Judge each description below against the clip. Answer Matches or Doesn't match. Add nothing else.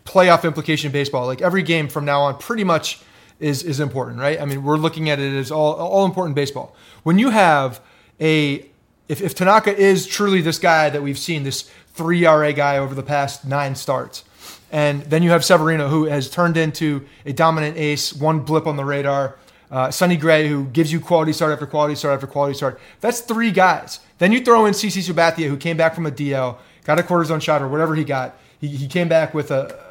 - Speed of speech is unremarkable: Doesn't match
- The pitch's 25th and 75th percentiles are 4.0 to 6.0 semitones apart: Doesn't match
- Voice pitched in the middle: Matches